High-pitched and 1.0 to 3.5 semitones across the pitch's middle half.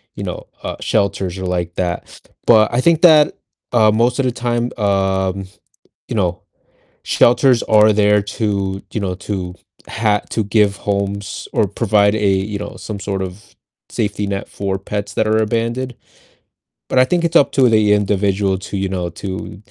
No: low, 105 Hz; narrow, 2.6 semitones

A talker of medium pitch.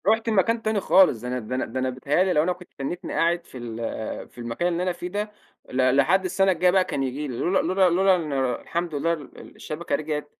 Yes: medium, 165 Hz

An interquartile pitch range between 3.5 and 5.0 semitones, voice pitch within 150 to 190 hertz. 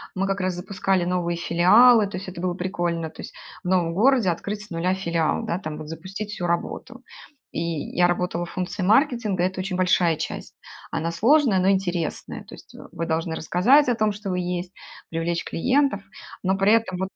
No: average, 2.8 semitones; medium, 185 Hz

